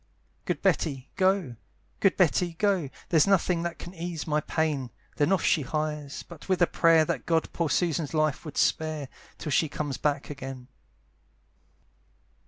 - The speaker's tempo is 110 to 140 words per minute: No, average, 160 wpm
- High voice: No, medium, 155 Hz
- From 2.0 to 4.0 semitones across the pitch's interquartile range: Yes, average, 2.9 semitones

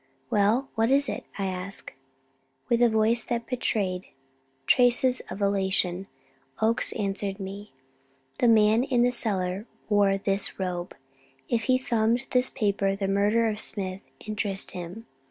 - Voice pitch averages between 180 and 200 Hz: No, high, 210 Hz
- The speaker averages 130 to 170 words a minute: Yes, average, 140 wpm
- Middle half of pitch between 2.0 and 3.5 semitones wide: Yes, average, 3.1 semitones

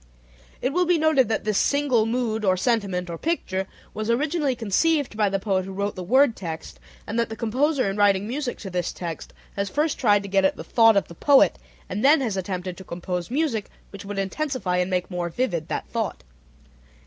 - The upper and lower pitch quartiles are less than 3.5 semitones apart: No, wide, 5.5 semitones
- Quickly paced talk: Yes, fast, 210 wpm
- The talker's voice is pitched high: Yes, high, 210 Hz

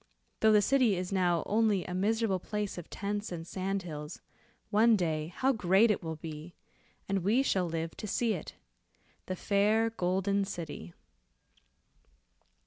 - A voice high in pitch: Yes, high, 195 Hz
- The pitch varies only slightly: No, average, 3.5 semitones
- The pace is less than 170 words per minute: Yes, average, 150 wpm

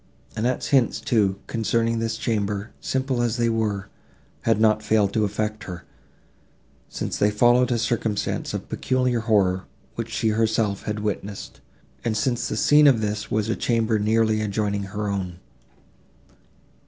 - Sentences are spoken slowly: No, average, 150 wpm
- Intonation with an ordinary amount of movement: No, narrow, 1.9 semitones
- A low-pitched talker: Yes, low, 110 Hz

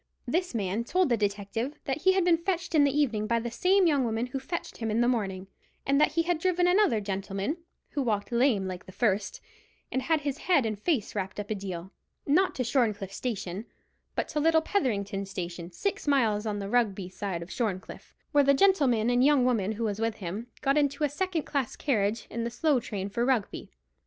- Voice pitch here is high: Yes, high, 235 Hz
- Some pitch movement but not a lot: No, wide, 6.4 semitones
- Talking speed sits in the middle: No, fast, 215 wpm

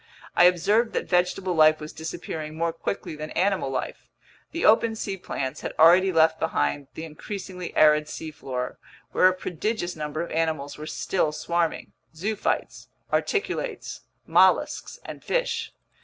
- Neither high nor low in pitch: Yes, medium, 165 Hz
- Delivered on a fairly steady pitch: No, average, 3.4 semitones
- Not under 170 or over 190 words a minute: No, average, 140 wpm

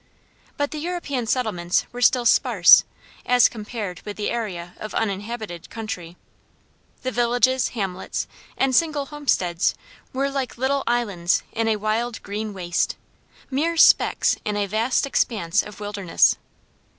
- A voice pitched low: No, high, 225 Hz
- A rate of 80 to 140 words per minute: Yes, slow, 135 wpm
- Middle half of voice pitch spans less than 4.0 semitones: No, average, 4.3 semitones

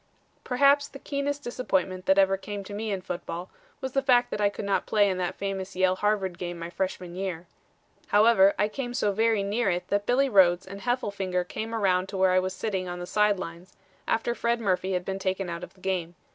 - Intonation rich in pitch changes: No, average, 3.1 semitones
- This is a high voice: Yes, high, 195 Hz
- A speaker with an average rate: No, fast, 225 wpm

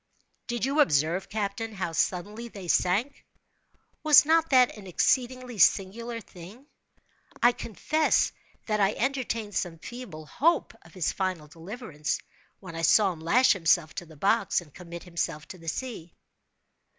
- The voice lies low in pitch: No, high, 200 Hz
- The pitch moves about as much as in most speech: No, wide, 6.1 semitones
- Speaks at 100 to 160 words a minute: Yes, average, 150 wpm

